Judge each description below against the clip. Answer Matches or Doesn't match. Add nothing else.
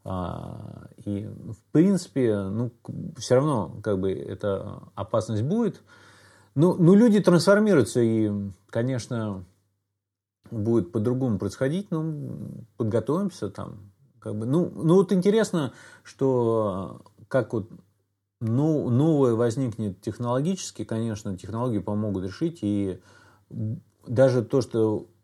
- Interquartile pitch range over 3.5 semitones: Matches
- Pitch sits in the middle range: Doesn't match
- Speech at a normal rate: Doesn't match